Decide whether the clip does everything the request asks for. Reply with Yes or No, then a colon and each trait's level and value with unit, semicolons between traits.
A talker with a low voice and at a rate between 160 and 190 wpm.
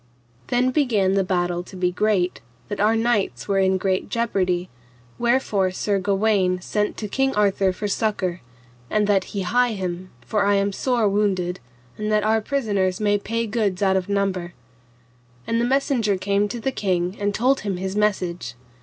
No: high, 200 Hz; average, 175 wpm